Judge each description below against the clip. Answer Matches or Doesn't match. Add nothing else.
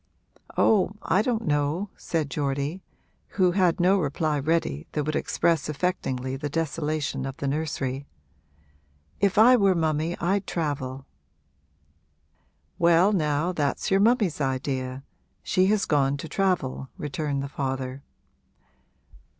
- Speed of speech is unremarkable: Doesn't match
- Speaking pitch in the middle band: Matches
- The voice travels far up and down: Doesn't match